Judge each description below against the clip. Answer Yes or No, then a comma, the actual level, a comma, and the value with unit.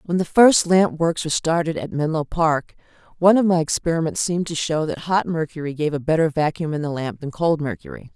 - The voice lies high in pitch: No, medium, 160 Hz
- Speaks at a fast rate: Yes, fast, 220 wpm